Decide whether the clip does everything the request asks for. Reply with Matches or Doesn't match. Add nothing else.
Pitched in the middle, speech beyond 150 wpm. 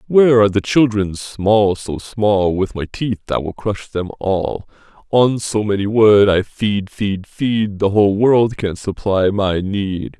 Doesn't match